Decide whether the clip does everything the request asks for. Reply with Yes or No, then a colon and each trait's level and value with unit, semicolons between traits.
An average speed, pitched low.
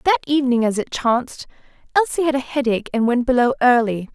No: average, 190 wpm; very high, 260 Hz